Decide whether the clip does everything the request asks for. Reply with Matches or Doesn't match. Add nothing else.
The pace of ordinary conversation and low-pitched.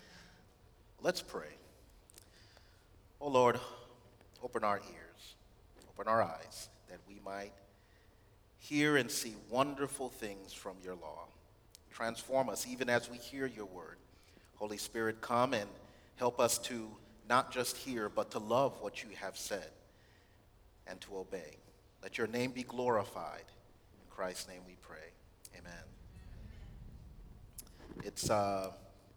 Doesn't match